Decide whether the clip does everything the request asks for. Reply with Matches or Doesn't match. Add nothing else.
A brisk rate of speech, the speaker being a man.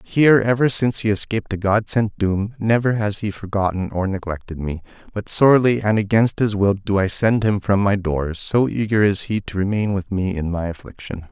Matches